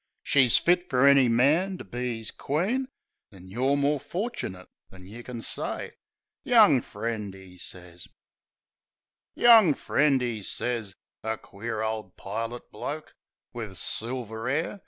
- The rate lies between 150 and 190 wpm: No, slow, 135 wpm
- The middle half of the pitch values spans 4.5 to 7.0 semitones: Yes, average, 5.2 semitones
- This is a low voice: Yes, low, 120 Hz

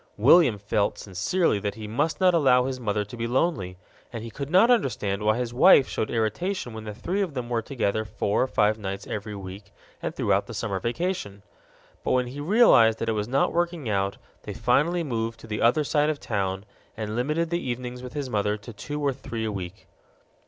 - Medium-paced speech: No, fast, 215 wpm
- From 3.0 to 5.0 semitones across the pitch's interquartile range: No, wide, 5.6 semitones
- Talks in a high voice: No, low, 115 Hz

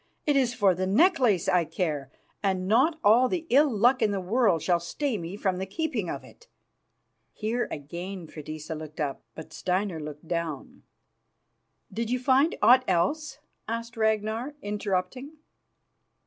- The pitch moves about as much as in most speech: No, wide, 6.4 semitones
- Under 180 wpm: Yes, average, 150 wpm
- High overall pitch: Yes, high, 205 Hz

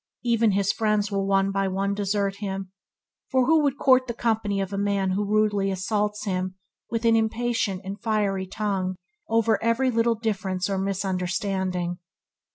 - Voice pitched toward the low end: No, high, 200 Hz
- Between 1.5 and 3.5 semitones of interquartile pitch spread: Yes, narrow, 2.6 semitones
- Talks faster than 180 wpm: No, average, 165 wpm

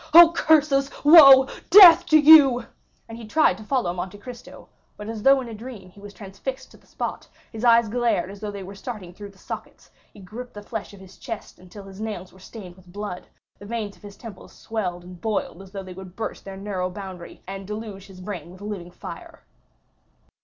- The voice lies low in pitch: No, high, 205 Hz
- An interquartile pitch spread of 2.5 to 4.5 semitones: Yes, average, 4.1 semitones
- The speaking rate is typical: No, fast, 210 wpm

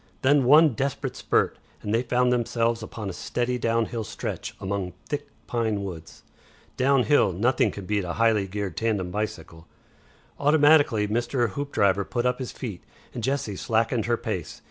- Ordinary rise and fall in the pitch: Yes, average, 3.6 semitones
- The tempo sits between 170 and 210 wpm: No, average, 155 wpm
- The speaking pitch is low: Yes, low, 115 Hz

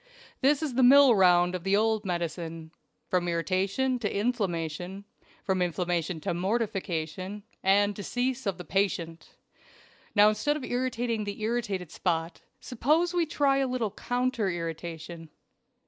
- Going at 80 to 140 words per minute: Yes, slow, 135 wpm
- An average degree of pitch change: No, wide, 5.8 semitones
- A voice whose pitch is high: Yes, high, 200 Hz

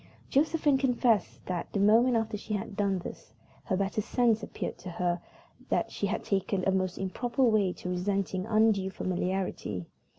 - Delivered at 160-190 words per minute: Yes, average, 170 wpm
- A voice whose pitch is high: Yes, high, 200 Hz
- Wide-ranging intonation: No, average, 3.3 semitones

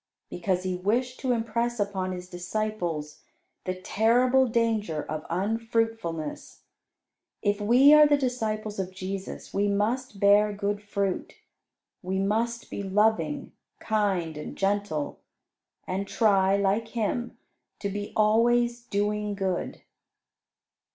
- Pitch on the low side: No, high, 205 Hz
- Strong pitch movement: No, average, 3.1 semitones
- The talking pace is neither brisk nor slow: No, slow, 115 wpm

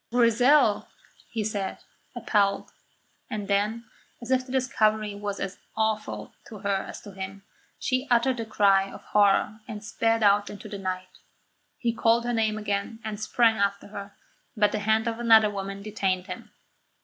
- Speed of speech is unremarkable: Yes, average, 165 wpm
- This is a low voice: No, high, 215 Hz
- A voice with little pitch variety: Yes, narrow, 2.3 semitones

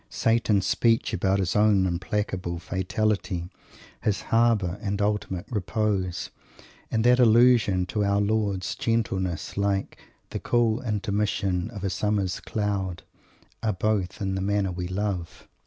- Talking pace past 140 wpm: No, slow, 135 wpm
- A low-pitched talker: Yes, low, 100 Hz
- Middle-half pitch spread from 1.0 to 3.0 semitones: Yes, narrow, 2.5 semitones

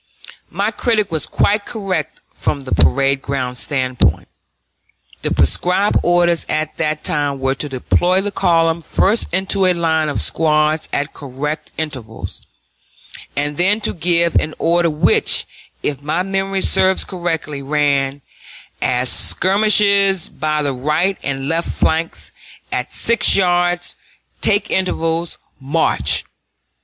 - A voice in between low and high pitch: Yes, medium, 160 Hz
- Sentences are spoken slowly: Yes, slow, 125 wpm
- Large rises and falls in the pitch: No, average, 4.5 semitones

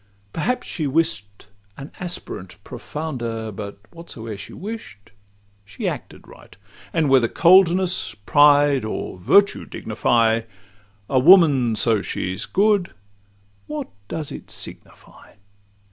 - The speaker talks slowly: Yes, slow, 115 wpm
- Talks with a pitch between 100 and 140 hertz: Yes, low, 135 Hz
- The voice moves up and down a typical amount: No, wide, 7.2 semitones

